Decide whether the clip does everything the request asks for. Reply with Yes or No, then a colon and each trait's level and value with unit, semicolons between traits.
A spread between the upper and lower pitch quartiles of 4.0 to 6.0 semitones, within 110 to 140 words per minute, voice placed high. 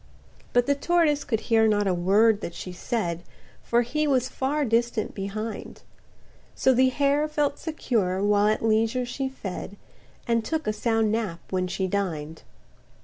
No: average, 4.7 semitones; average, 160 wpm; high, 225 Hz